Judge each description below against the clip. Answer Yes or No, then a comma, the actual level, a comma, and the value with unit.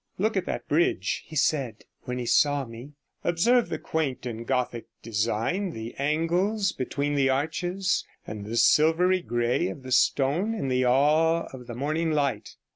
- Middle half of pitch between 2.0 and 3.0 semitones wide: No, average, 5.1 semitones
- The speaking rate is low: No, average, 165 wpm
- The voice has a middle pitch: Yes, medium, 145 Hz